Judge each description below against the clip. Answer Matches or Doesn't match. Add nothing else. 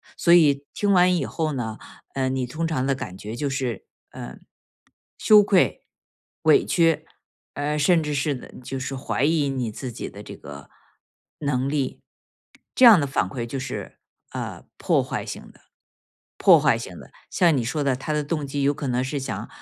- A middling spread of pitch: Matches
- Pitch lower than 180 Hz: Matches